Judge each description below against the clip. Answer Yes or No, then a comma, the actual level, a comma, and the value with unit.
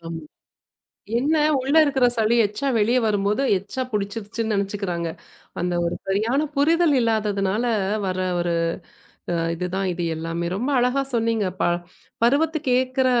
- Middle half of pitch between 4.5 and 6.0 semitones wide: Yes, average, 5.0 semitones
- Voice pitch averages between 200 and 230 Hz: Yes, high, 215 Hz